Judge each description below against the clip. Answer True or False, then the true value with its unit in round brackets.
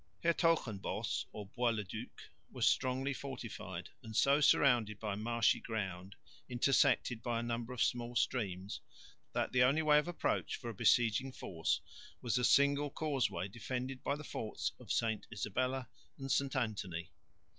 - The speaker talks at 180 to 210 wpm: False (155 wpm)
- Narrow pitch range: False (4.1 semitones)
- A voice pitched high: False (120 Hz)